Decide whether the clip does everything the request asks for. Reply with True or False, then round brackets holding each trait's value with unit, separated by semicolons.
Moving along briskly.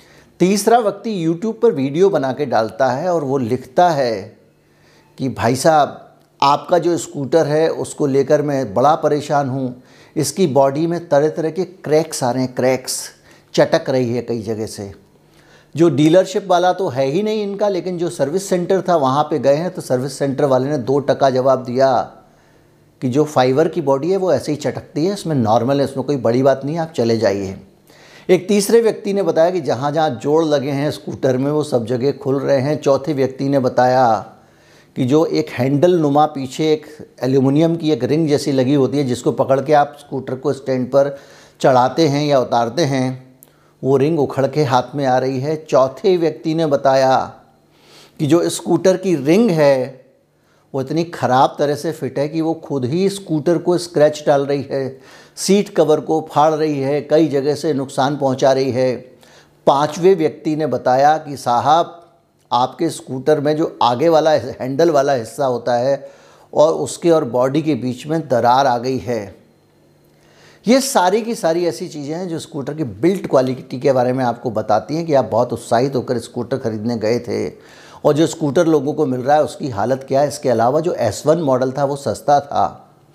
True (195 wpm)